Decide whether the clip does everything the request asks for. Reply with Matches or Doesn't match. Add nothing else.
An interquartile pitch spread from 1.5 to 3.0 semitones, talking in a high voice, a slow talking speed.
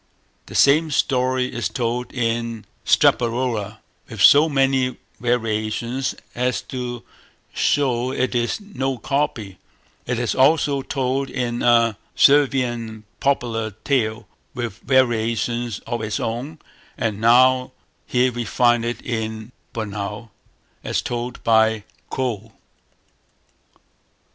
Doesn't match